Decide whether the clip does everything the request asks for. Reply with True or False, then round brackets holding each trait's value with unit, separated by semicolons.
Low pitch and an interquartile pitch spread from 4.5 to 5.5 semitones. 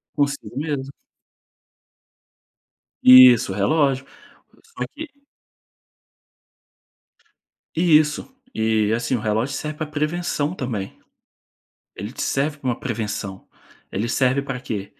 True (130 Hz; 5.1 semitones)